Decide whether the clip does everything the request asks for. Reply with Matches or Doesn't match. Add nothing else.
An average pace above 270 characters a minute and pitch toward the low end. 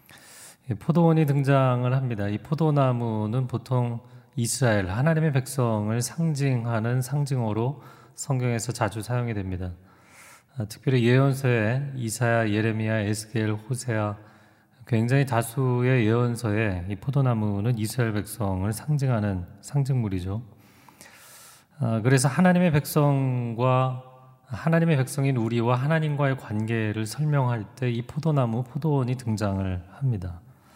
Matches